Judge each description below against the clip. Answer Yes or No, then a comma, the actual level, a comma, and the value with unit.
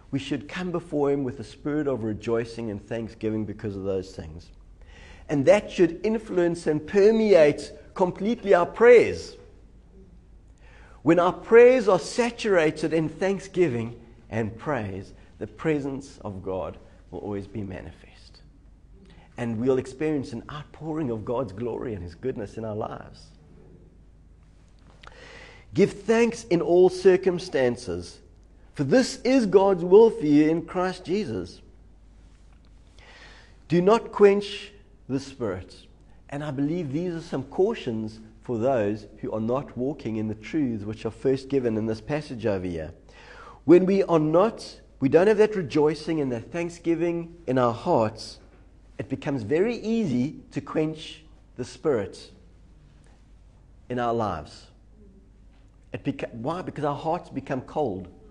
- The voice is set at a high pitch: No, low, 130 Hz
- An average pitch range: No, wide, 8.6 semitones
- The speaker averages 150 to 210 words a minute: No, average, 140 wpm